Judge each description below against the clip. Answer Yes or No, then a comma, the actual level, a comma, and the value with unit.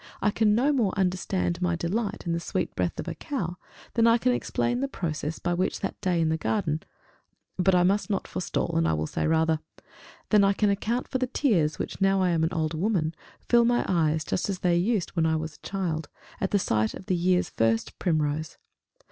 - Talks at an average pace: No, fast, 215 wpm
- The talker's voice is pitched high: No, medium, 180 Hz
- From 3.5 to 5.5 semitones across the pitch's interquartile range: Yes, average, 4.4 semitones